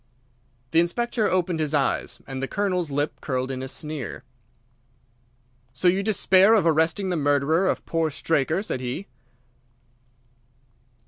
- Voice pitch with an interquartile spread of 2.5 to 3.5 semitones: No, average, 4.9 semitones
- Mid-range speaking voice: Yes, medium, 160 Hz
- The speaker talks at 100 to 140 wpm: Yes, slow, 135 wpm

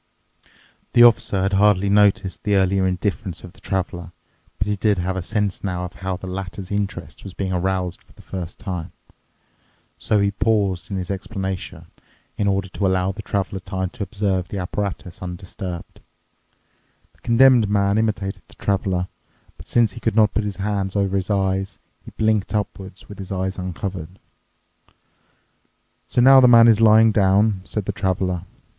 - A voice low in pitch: Yes, very low, 95 Hz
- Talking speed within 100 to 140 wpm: No, average, 170 wpm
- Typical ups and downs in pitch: No, narrow, 1.8 semitones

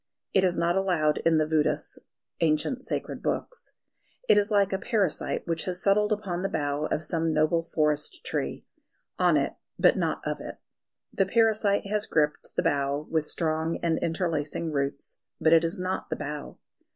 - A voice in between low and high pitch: Yes, medium, 165 Hz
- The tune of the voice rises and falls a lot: No, average, 4.0 semitones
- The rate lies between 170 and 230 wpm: Yes, average, 175 wpm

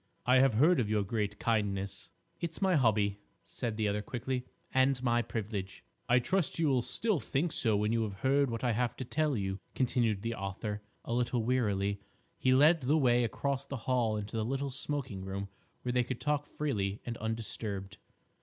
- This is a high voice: No, low, 120 Hz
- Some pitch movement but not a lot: Yes, average, 4.2 semitones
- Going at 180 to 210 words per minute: Yes, average, 190 wpm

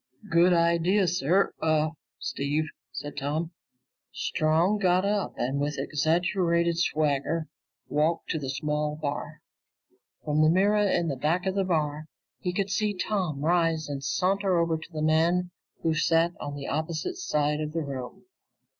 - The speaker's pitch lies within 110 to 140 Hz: No, medium, 160 Hz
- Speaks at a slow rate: No, average, 155 wpm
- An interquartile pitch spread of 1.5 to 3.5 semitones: Yes, average, 3.1 semitones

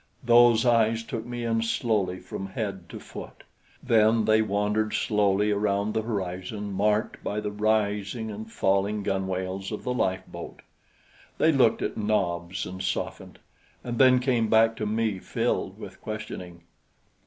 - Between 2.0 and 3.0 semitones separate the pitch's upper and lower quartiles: Yes, narrow, 2.6 semitones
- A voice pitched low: Yes, low, 105 Hz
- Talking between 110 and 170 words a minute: Yes, average, 145 wpm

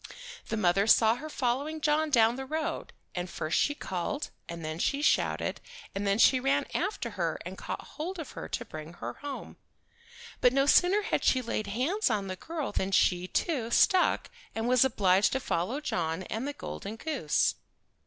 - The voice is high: Yes, high, 245 Hz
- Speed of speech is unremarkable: Yes, average, 185 wpm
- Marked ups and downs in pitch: Yes, wide, 7.2 semitones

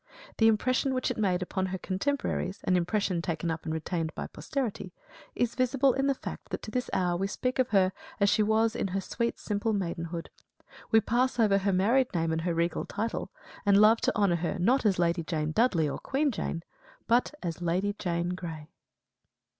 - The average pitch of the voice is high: Yes, high, 195 Hz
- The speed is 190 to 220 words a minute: Yes, average, 195 wpm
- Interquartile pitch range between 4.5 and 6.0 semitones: Yes, average, 5.0 semitones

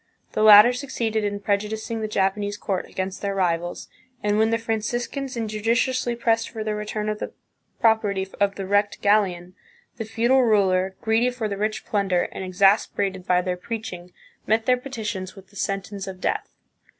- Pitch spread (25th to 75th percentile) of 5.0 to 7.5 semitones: No, narrow, 2.6 semitones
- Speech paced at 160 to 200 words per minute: Yes, average, 170 wpm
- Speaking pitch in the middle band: No, high, 210 Hz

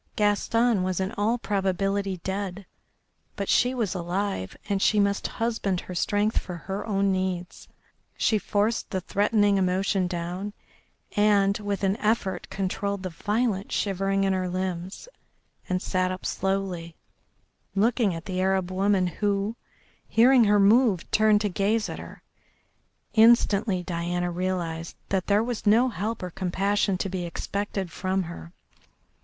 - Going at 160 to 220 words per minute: No, average, 145 wpm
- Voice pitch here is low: No, high, 195 Hz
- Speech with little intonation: Yes, narrow, 2.1 semitones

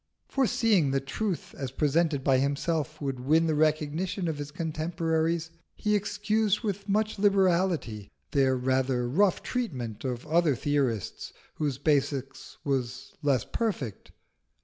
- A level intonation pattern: No, wide, 5.6 semitones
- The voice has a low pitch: No, medium, 155 Hz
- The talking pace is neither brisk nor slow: No, slow, 125 wpm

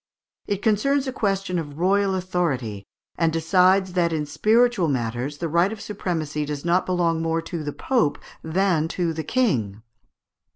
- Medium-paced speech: Yes, average, 160 wpm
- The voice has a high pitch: No, medium, 170 Hz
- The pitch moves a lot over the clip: No, average, 4.3 semitones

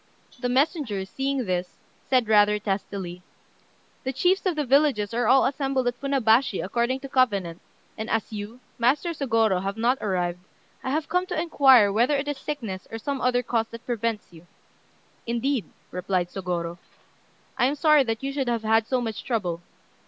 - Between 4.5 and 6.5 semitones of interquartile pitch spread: Yes, average, 4.9 semitones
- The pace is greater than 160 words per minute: Yes, average, 175 wpm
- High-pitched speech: Yes, high, 235 Hz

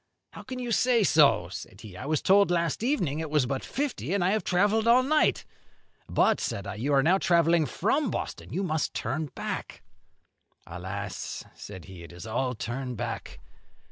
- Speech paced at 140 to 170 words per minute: No, average, 185 wpm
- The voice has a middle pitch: Yes, medium, 155 Hz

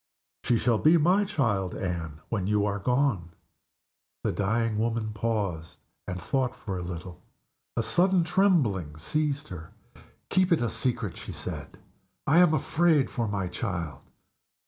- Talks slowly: No, average, 145 wpm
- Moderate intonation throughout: No, wide, 7.8 semitones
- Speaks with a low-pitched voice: Yes, low, 110 Hz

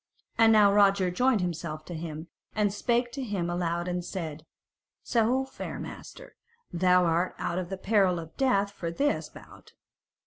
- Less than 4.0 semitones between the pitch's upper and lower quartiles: No, average, 4.4 semitones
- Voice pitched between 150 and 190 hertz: Yes, medium, 185 Hz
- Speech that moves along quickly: No, average, 165 wpm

